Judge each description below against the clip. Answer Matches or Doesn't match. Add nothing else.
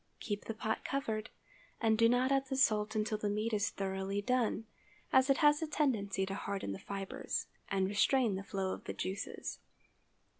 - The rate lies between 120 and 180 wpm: Doesn't match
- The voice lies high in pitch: Matches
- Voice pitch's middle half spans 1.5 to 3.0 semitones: Doesn't match